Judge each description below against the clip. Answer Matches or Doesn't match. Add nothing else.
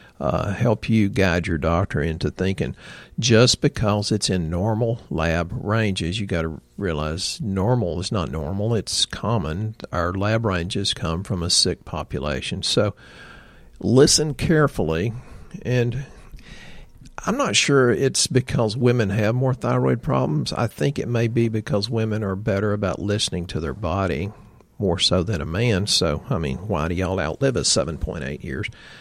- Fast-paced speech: Doesn't match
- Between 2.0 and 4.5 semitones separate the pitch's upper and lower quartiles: Doesn't match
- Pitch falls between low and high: Doesn't match